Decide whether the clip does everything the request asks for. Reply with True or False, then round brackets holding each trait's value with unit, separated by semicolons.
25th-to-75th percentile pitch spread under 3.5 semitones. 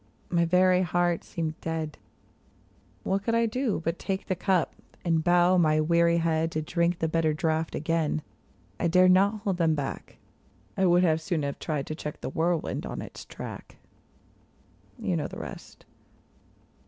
True (2.4 semitones)